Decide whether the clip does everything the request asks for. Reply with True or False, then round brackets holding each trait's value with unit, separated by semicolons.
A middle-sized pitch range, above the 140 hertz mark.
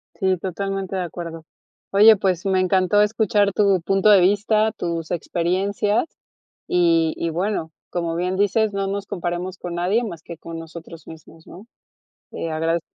True (3.0 semitones; 185 Hz)